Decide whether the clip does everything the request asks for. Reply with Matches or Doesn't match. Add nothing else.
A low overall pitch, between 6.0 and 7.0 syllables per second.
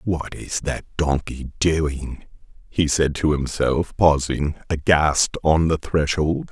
Doesn't match